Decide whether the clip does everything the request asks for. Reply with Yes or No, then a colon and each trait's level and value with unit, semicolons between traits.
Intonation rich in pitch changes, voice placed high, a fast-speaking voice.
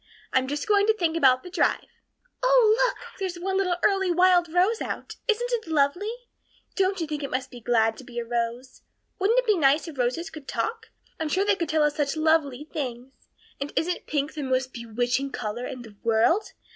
Yes: wide, 6.8 semitones; very high, 310 Hz; fast, 210 wpm